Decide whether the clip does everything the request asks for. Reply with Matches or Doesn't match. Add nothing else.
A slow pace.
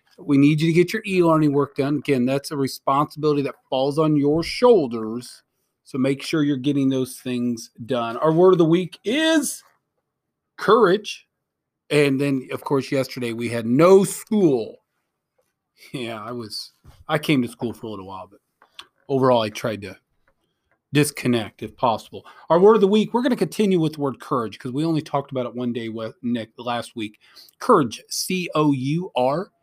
Doesn't match